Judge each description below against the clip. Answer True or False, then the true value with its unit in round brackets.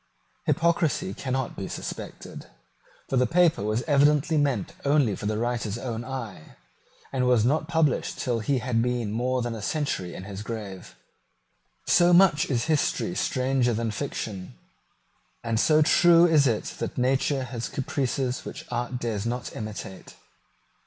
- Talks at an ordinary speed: True (150 wpm)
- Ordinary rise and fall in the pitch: True (4.2 semitones)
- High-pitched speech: False (125 Hz)